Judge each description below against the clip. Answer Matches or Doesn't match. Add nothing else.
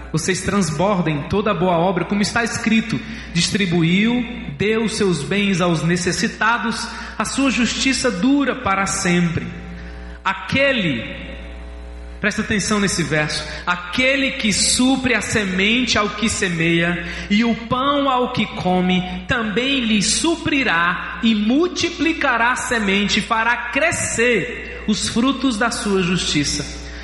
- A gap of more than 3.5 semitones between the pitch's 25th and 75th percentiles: Matches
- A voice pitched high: Matches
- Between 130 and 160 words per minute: Doesn't match